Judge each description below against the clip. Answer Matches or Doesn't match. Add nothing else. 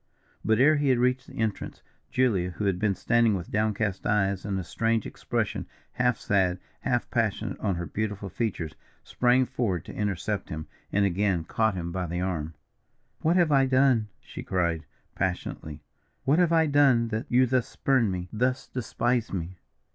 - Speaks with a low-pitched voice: Matches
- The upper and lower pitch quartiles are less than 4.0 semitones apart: Doesn't match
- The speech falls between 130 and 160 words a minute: Doesn't match